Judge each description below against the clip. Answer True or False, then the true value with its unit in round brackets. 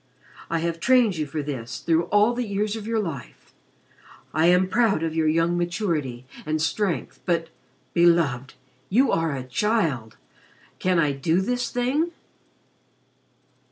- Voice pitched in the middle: True (170 Hz)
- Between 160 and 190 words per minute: False (145 wpm)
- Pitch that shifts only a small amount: False (5.2 semitones)